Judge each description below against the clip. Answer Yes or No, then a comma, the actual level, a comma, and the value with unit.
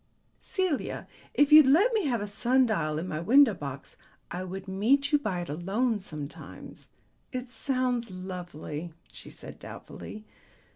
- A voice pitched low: No, high, 215 Hz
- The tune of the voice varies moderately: No, wide, 7.0 semitones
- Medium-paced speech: Yes, average, 150 wpm